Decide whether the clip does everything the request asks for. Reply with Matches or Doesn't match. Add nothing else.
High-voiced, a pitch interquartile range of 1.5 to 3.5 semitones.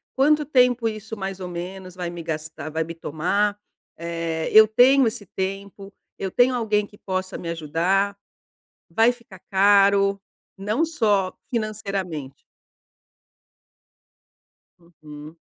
Doesn't match